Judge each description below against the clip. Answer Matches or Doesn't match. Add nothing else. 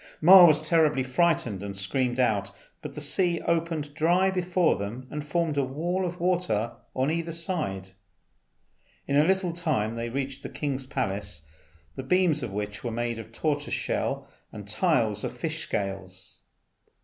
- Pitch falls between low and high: Matches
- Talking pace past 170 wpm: Doesn't match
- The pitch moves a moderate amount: Doesn't match